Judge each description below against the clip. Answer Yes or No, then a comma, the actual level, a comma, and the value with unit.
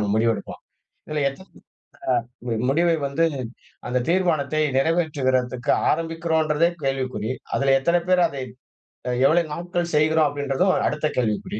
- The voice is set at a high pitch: No, medium, 150 Hz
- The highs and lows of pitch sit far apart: No, average, 3.7 semitones